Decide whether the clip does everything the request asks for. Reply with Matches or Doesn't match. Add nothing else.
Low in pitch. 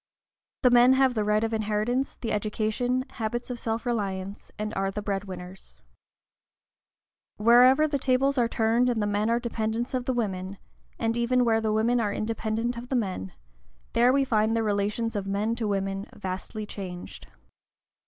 Doesn't match